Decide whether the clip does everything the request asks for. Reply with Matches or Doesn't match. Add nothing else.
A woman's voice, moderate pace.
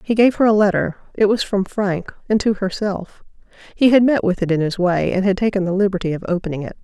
Doesn't match